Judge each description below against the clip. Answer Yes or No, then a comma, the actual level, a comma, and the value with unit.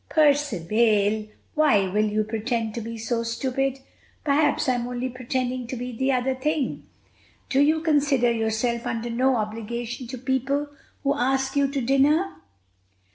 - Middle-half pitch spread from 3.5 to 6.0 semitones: No, average, 3.1 semitones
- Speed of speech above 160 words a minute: No, average, 145 wpm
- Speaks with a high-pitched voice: Yes, very high, 250 Hz